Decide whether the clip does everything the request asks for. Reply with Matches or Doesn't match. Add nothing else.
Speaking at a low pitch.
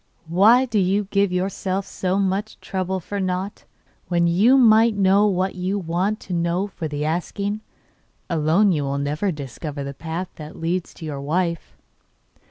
Doesn't match